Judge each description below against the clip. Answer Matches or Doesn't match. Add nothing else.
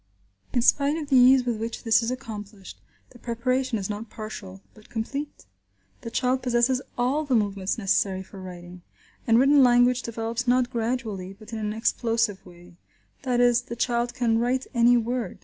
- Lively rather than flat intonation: Doesn't match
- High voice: Matches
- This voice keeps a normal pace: Matches